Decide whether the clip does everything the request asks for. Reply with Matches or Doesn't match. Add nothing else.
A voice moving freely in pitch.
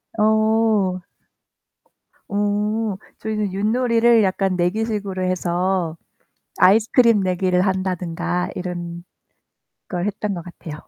Doesn't match